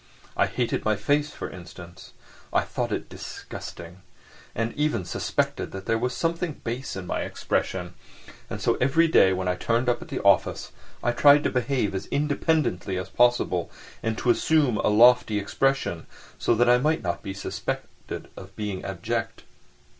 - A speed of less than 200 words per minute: Yes, average, 170 wpm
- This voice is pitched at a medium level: No, low, 115 Hz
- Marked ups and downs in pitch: Yes, wide, 6.1 semitones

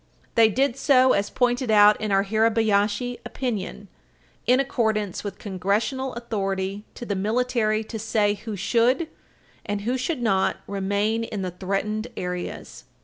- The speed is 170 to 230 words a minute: No, average, 145 wpm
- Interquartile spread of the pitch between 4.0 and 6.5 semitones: No, average, 3.2 semitones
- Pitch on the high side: Yes, high, 215 Hz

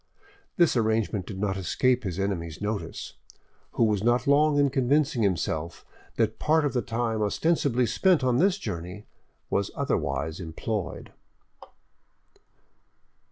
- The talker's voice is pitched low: Yes, low, 110 Hz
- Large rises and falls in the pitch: Yes, wide, 5.8 semitones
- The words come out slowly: Yes, slow, 125 wpm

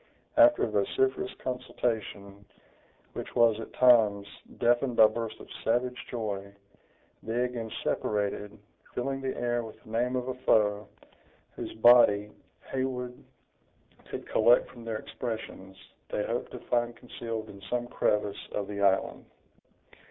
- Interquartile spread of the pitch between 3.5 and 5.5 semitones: No, average, 3.0 semitones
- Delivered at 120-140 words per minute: Yes, slow, 135 wpm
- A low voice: Yes, low, 115 Hz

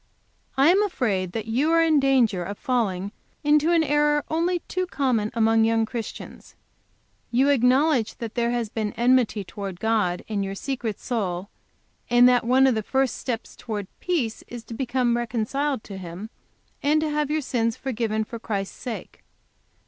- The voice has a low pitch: No, high, 240 Hz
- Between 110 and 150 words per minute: No, average, 170 wpm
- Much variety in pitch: No, average, 4.0 semitones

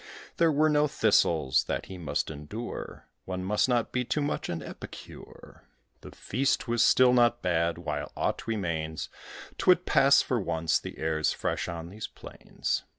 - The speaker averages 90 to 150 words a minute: No, average, 160 wpm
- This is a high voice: No, low, 105 Hz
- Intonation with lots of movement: Yes, wide, 7.5 semitones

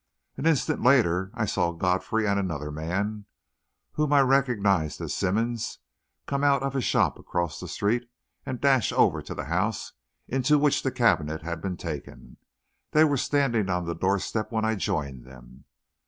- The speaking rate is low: No, average, 170 wpm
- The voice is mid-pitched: No, low, 105 Hz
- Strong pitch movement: Yes, wide, 7.1 semitones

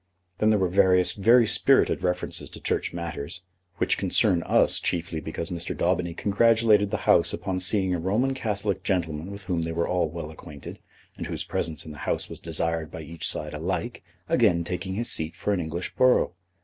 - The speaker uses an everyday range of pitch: Yes, average, 3.4 semitones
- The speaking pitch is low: Yes, very low, 90 Hz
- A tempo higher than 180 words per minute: Yes, average, 190 wpm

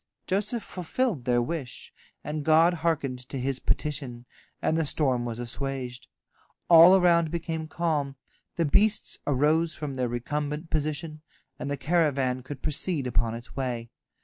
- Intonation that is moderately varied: Yes, average, 4.4 semitones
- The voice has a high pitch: No, medium, 150 Hz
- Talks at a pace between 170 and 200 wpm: No, average, 145 wpm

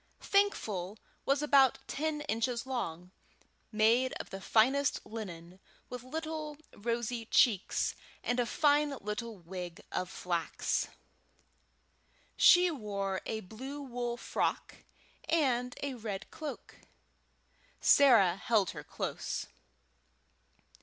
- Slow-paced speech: Yes, slow, 105 wpm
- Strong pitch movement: Yes, wide, 5.7 semitones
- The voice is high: Yes, high, 235 Hz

